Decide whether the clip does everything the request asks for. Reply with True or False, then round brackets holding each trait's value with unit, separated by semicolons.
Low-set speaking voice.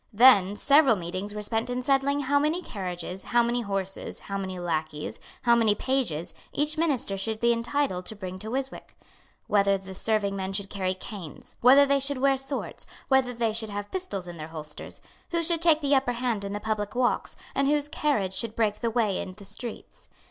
False (220 Hz)